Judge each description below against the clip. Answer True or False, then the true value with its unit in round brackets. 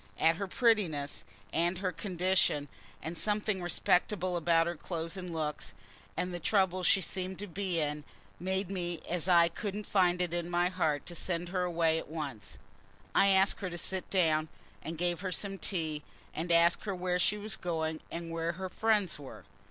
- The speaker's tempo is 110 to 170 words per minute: False (185 wpm)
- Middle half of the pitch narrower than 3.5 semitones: True (2.4 semitones)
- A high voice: False (175 Hz)